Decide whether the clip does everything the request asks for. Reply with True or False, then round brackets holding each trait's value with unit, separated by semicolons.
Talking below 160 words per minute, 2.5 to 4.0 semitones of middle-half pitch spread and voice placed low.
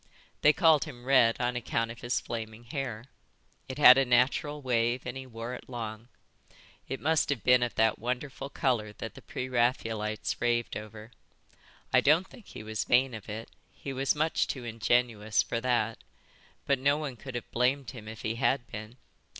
False (185 wpm; 2.9 semitones; 120 Hz)